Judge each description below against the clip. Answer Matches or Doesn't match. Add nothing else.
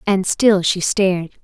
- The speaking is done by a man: Doesn't match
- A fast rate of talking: Doesn't match